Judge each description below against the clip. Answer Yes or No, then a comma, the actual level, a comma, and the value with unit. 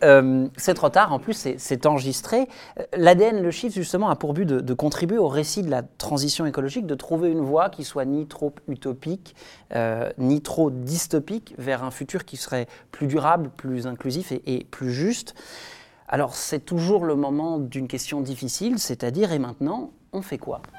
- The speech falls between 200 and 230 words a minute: No, average, 185 wpm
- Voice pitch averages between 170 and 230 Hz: No, medium, 145 Hz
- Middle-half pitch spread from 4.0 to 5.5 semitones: Yes, average, 4.6 semitones